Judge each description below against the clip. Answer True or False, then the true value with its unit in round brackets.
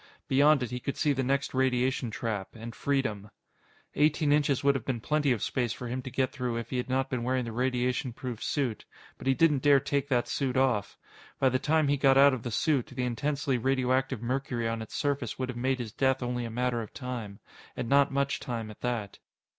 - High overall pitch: False (130 Hz)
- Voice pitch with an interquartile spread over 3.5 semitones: False (2.4 semitones)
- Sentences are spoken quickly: True (225 wpm)